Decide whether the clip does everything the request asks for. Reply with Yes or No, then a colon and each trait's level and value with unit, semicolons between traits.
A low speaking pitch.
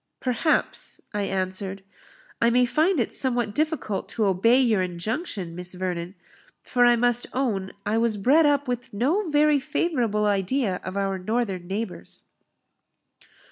No: high, 225 Hz